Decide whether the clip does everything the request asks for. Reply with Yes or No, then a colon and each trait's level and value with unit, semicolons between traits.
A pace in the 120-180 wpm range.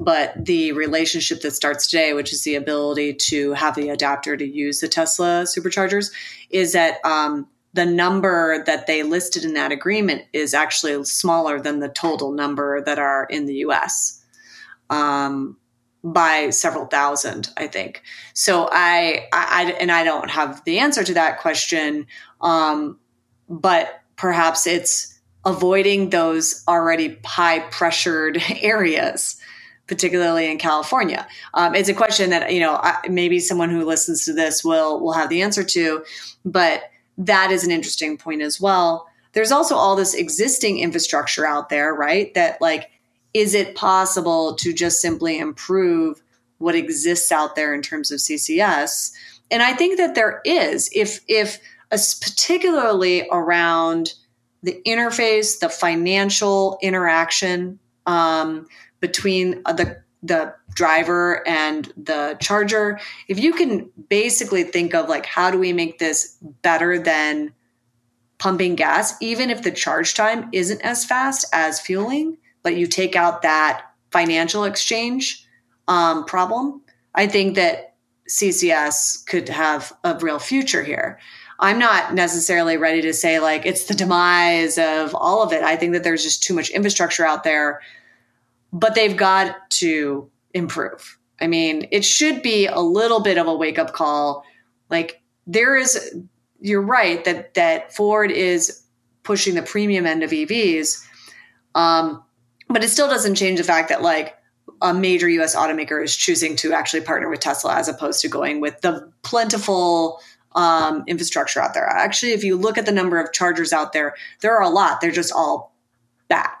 Yes: average, 155 wpm